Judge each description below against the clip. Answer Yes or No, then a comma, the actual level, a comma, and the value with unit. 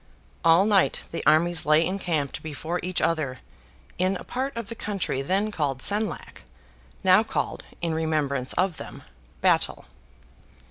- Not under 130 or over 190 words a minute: Yes, average, 140 wpm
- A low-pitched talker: No, medium, 170 Hz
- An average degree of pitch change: Yes, average, 4.1 semitones